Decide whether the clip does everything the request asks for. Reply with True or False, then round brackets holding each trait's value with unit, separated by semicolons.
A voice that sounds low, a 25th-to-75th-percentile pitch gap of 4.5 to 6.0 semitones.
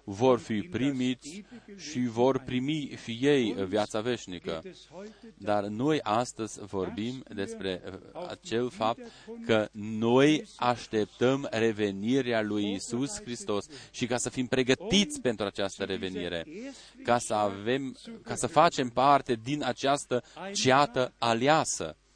True (125 Hz; 4.8 semitones)